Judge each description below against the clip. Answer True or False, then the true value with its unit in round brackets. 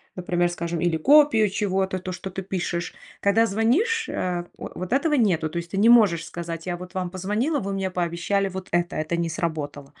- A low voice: False (185 Hz)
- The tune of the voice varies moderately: True (3.1 semitones)